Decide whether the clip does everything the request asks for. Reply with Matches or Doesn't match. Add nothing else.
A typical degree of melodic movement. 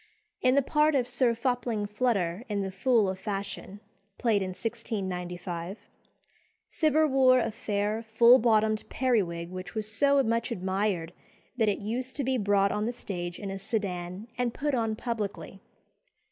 Matches